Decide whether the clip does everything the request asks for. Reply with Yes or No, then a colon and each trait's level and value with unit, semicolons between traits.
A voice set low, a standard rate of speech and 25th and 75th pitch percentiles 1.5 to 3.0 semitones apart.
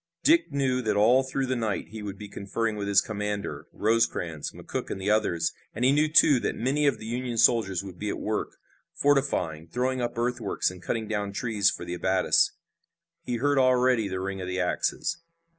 No: low, 110 Hz; average, 195 wpm; average, 4.4 semitones